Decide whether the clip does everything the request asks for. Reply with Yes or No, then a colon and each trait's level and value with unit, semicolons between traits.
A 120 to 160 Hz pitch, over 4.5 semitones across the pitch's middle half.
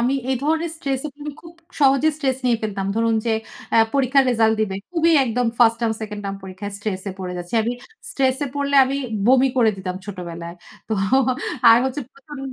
No: high, 240 Hz; average, 5.0 semitones